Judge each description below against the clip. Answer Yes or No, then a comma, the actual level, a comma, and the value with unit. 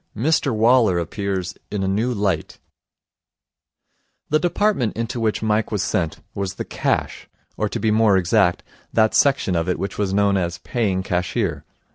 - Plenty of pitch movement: No, average, 3.5 semitones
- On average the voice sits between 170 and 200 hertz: No, low, 100 Hz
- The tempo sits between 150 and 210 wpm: Yes, average, 160 wpm